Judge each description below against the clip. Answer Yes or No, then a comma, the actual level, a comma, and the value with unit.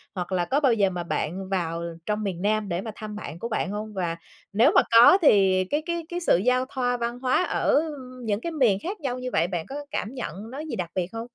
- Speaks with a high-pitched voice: Yes, high, 215 Hz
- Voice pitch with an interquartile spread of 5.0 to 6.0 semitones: Yes, wide, 5.5 semitones